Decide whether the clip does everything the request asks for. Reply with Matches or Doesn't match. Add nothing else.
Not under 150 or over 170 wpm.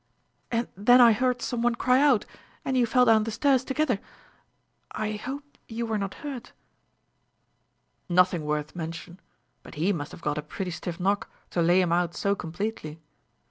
Doesn't match